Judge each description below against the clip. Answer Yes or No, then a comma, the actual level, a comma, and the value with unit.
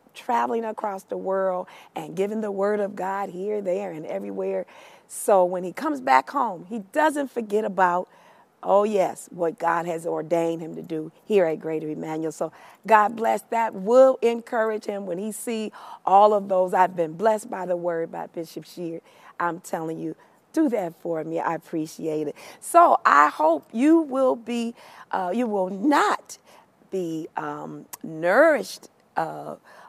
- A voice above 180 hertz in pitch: Yes, high, 190 Hz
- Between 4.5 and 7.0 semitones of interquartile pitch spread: Yes, average, 5.2 semitones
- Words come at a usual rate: Yes, average, 165 wpm